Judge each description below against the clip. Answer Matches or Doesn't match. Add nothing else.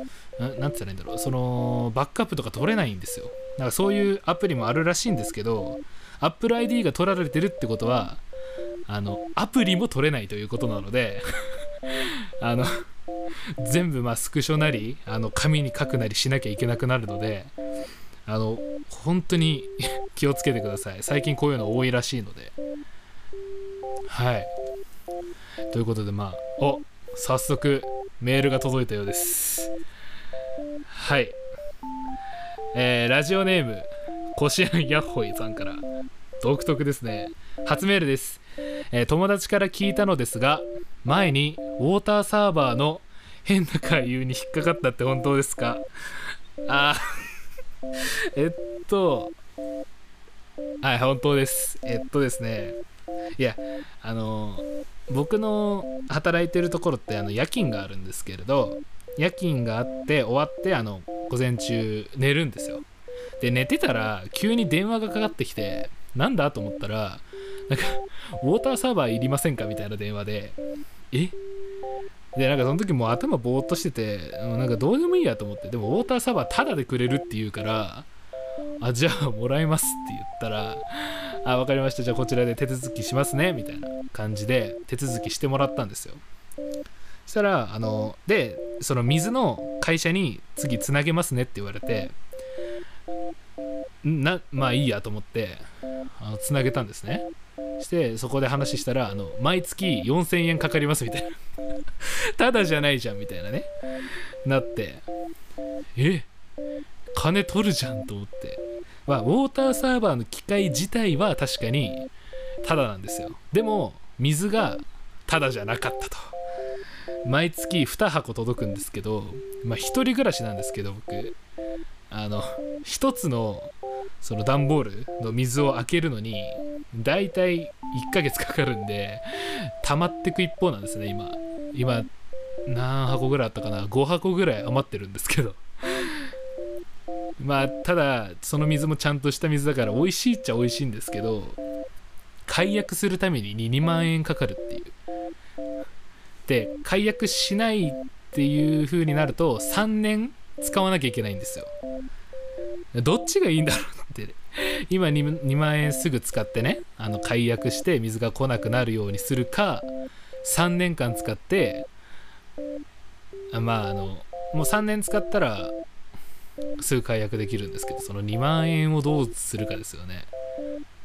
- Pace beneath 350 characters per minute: Matches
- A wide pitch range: Matches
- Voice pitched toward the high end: Doesn't match